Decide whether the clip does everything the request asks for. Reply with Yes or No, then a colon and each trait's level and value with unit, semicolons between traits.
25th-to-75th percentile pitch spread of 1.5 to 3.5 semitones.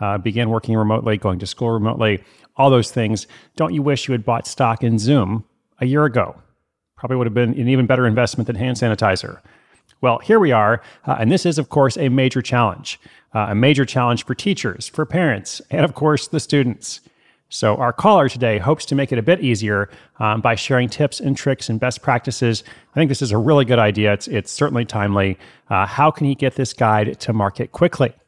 No: average, 3.9 semitones